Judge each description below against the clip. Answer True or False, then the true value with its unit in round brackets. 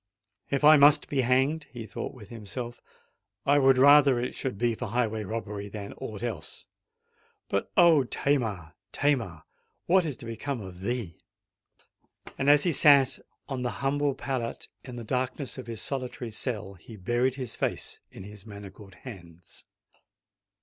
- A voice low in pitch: True (120 Hz)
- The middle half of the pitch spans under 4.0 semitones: False (4.6 semitones)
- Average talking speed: True (155 wpm)